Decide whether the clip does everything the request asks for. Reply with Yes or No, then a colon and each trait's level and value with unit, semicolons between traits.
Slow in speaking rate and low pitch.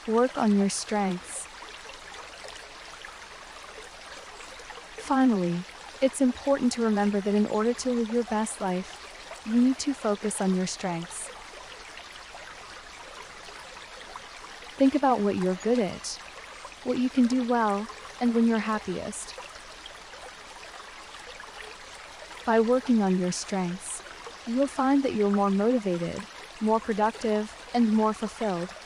No: slow, 115 wpm; high, 220 Hz